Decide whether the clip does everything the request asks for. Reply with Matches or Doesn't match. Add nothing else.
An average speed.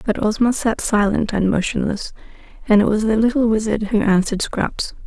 Matches